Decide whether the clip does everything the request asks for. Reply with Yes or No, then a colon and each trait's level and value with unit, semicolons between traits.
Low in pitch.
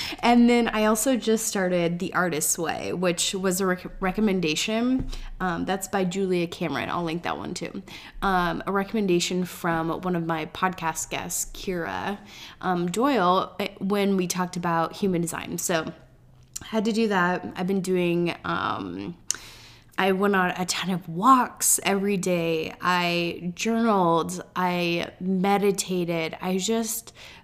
No: medium, 180 Hz